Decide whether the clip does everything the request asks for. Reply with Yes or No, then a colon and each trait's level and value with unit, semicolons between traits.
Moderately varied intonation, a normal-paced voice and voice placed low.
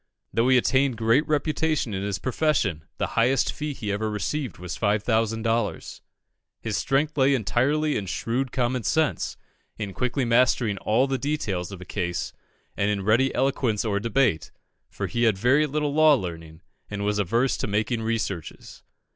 Yes: average, 4.8 semitones; average, 165 wpm; low, 115 Hz